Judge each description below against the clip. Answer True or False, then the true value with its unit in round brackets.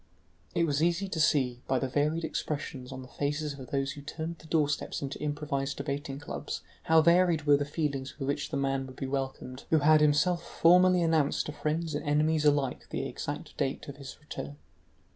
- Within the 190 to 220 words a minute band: True (200 wpm)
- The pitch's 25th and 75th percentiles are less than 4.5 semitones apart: True (2.5 semitones)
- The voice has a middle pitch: True (145 Hz)